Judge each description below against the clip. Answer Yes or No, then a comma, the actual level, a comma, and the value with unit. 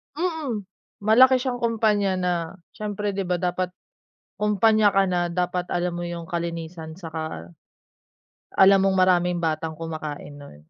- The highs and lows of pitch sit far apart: No, average, 3.8 semitones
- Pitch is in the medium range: Yes, medium, 180 Hz